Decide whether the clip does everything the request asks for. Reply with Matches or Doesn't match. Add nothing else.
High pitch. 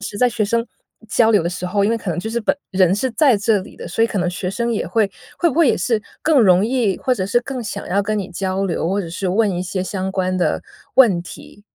Matches